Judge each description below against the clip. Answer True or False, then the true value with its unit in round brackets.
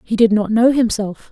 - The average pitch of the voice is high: True (220 Hz)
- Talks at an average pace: False (230 wpm)